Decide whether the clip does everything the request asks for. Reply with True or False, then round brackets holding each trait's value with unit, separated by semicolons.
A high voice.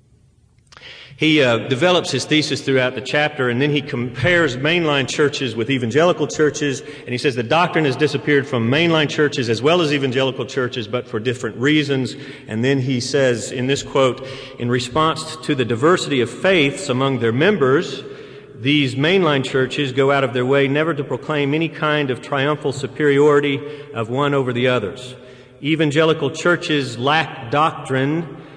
False (140 Hz)